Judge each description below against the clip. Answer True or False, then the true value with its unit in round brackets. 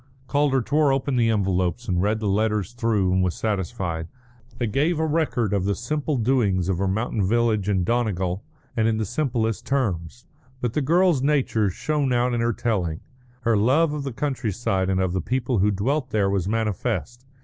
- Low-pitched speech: True (115 Hz)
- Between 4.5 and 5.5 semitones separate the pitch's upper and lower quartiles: True (5.1 semitones)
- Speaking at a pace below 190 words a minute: False (195 wpm)